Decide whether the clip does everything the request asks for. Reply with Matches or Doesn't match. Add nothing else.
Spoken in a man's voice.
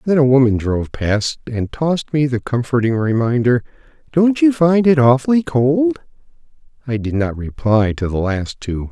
Matches